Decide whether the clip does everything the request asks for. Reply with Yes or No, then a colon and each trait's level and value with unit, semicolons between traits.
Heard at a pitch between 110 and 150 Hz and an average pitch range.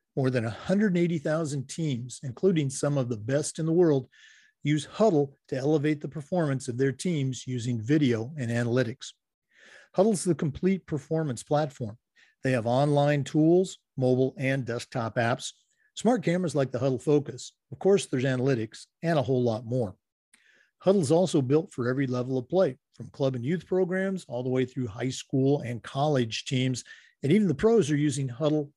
Yes: medium, 140 Hz; average, 4.1 semitones